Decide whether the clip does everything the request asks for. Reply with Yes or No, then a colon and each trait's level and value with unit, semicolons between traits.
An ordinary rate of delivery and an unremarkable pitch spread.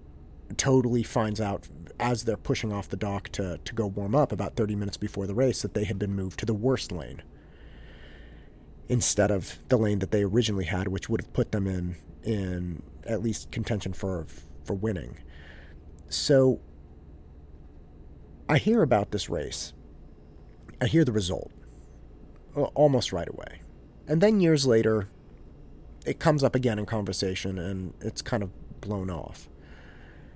No: average, 160 wpm; wide, 6.6 semitones